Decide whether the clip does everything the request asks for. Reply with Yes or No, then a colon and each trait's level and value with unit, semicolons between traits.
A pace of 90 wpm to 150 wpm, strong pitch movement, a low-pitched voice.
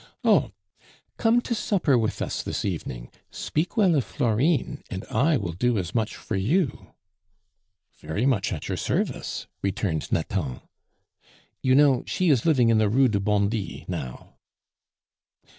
Yes: average, 145 wpm; wide, 6.8 semitones; low, 115 Hz